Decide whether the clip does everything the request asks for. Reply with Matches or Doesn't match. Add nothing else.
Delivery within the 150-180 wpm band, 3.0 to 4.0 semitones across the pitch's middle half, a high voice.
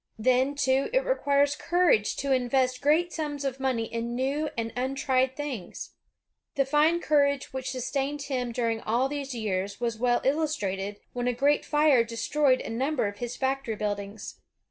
Matches